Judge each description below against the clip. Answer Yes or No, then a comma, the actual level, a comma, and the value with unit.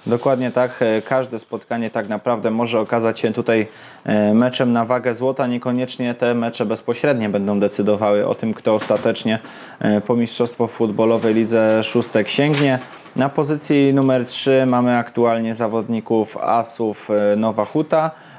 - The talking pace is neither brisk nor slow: Yes, average, 130 wpm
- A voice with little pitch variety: Yes, narrow, 2.2 semitones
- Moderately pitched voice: No, low, 115 Hz